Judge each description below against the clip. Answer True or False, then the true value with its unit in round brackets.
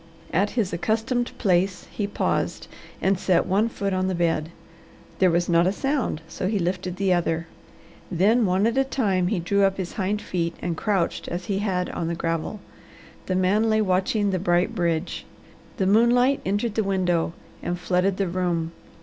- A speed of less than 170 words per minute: False (185 wpm)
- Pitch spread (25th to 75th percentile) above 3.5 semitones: False (2.8 semitones)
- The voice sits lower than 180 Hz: False (185 Hz)